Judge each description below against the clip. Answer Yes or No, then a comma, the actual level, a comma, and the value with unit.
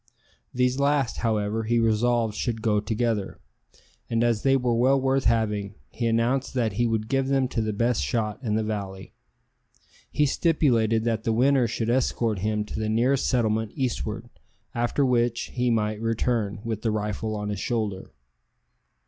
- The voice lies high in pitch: No, low, 115 Hz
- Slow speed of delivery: No, average, 165 wpm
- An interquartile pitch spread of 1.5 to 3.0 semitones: Yes, narrow, 2.4 semitones